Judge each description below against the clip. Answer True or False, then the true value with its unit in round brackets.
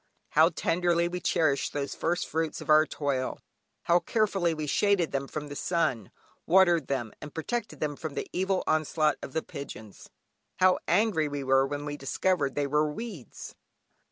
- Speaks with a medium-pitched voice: True (155 Hz)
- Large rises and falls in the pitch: False (3.5 semitones)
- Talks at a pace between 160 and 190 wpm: True (170 wpm)